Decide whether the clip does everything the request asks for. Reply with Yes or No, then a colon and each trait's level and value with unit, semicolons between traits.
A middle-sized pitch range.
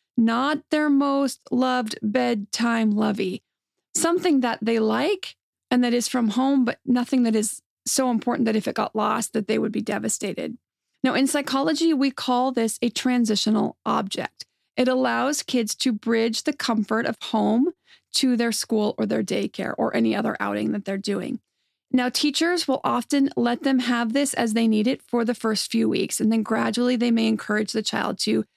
Yes: average, 3.3 semitones